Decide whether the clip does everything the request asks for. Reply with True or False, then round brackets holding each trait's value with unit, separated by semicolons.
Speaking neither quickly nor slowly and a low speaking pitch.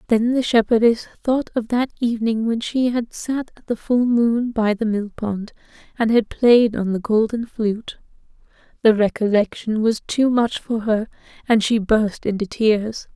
False (175 wpm; 225 Hz)